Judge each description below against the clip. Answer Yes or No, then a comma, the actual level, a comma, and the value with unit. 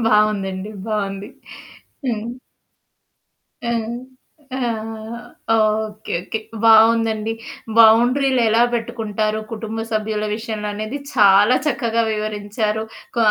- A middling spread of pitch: No, narrow, 1.3 semitones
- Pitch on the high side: Yes, high, 220 Hz